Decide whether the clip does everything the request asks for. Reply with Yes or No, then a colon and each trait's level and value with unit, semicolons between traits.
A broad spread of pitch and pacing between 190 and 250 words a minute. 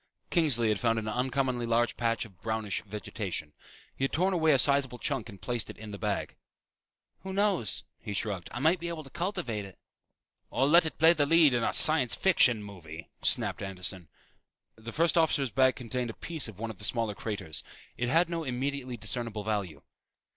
Yes: wide, 6.1 semitones; average, 195 wpm